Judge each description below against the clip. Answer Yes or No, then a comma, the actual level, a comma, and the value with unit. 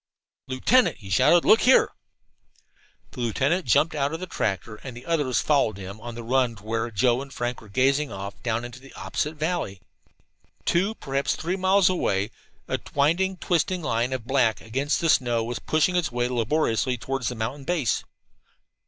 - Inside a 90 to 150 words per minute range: No, average, 180 wpm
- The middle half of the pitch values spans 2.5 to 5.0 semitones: No, wide, 5.5 semitones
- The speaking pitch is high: No, low, 130 Hz